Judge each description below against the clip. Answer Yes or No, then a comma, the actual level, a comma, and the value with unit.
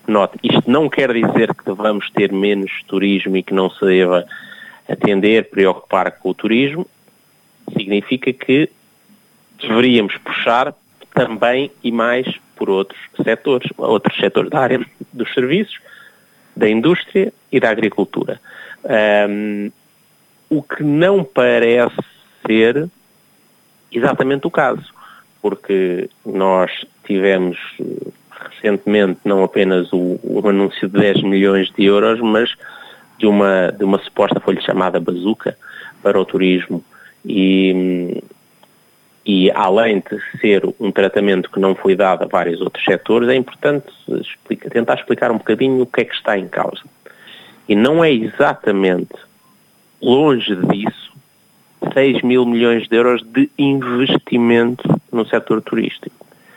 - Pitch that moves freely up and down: No, average, 4.2 semitones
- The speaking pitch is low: Yes, low, 105 Hz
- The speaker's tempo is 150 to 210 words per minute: No, average, 130 wpm